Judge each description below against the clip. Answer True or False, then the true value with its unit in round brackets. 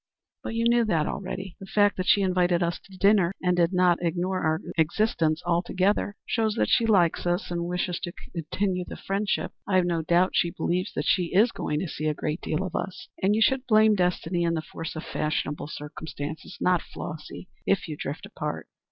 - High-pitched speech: False (180 Hz)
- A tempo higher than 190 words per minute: True (205 wpm)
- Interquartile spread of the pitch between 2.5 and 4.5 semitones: True (2.9 semitones)